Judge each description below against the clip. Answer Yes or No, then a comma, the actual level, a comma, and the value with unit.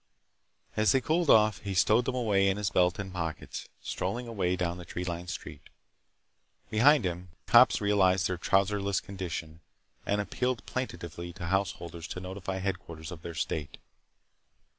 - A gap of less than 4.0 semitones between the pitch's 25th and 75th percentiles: Yes, average, 2.9 semitones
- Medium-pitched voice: No, very low, 95 Hz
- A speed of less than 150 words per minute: No, average, 155 wpm